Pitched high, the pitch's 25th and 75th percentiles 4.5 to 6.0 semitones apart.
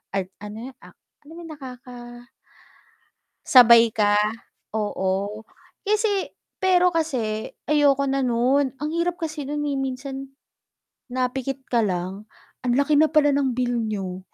Yes: very high, 260 Hz; average, 4.9 semitones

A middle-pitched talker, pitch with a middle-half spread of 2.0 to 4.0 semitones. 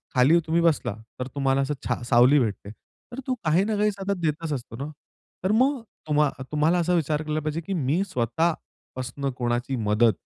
No: medium, 150 Hz; average, 5.0 semitones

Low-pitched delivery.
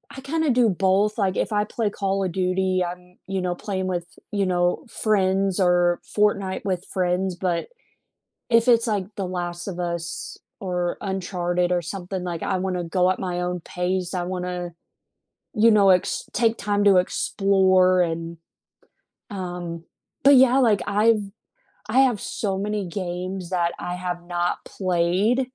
No: medium, 185 Hz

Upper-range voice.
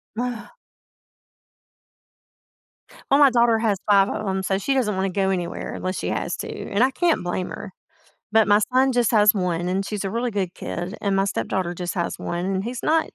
Yes: high, 200 Hz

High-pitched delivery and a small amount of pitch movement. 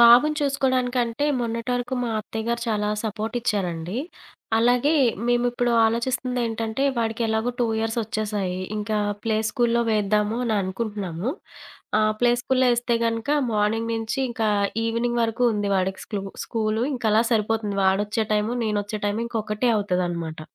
Yes: high, 225 Hz; narrow, 2.3 semitones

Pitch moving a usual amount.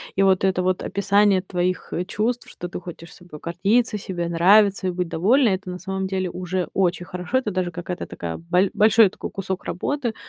No: narrow, 2.1 semitones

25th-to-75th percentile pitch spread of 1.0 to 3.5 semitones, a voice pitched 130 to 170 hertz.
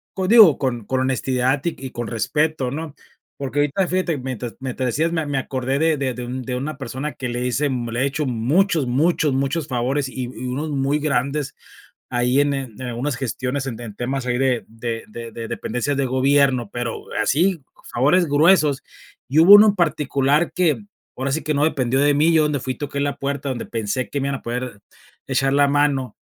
Yes: average, 3.0 semitones; low, 135 Hz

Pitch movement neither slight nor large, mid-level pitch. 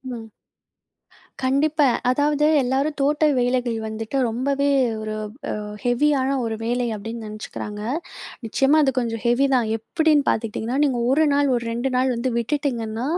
No: average, 3.7 semitones; very high, 255 Hz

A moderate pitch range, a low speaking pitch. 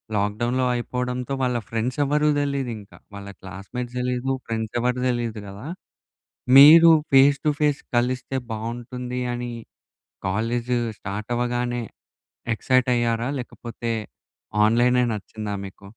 No: narrow, 2.1 semitones; low, 120 Hz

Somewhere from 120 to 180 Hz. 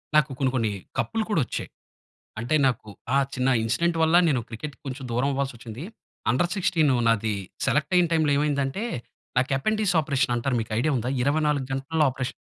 Yes: medium, 140 Hz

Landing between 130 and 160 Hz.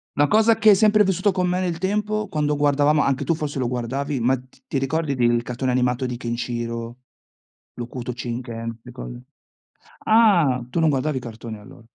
Yes: low, 135 Hz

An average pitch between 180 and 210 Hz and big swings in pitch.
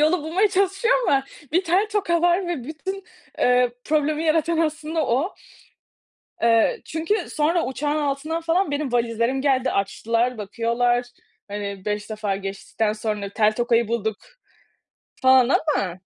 No: very high, 275 Hz; wide, 6.1 semitones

